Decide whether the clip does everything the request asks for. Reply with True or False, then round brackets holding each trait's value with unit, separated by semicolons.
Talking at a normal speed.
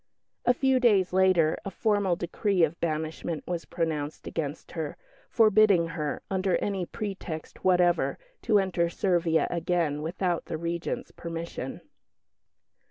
False (125 wpm)